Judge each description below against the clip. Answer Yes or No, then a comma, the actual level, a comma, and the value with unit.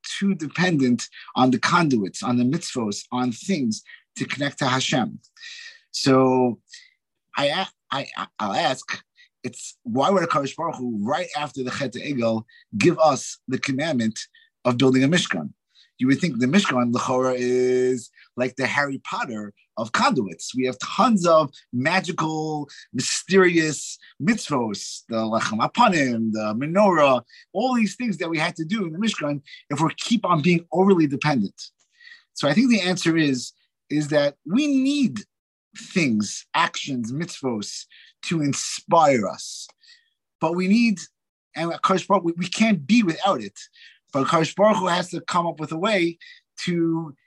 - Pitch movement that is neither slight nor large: No, wide, 8.1 semitones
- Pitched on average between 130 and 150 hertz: No, medium, 165 Hz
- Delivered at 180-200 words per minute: No, average, 150 wpm